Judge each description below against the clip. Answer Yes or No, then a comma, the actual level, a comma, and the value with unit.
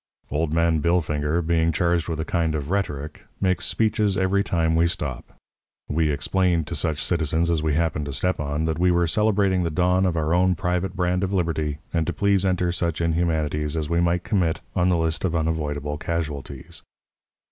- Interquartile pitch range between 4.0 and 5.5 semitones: No, narrow, 2.5 semitones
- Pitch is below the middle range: Yes, very low, 85 Hz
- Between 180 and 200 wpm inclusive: Yes, average, 190 wpm